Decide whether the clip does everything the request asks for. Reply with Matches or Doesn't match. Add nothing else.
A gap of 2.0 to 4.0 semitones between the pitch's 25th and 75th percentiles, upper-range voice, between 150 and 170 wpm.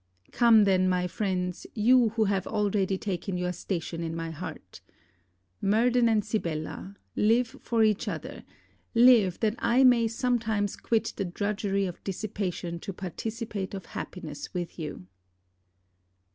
Doesn't match